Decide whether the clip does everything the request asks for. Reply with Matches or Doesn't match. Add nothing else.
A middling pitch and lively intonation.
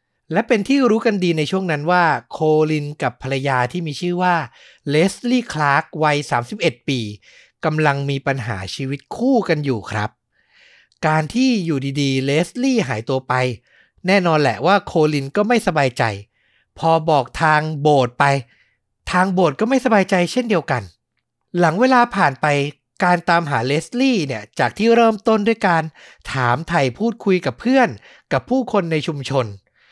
Matches